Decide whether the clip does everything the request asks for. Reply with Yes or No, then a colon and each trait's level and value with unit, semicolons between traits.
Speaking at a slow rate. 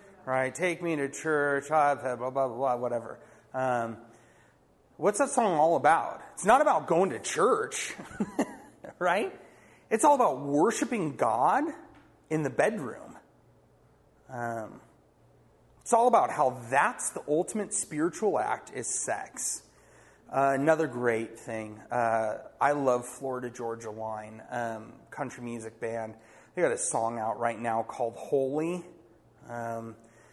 Yes: slow, 130 wpm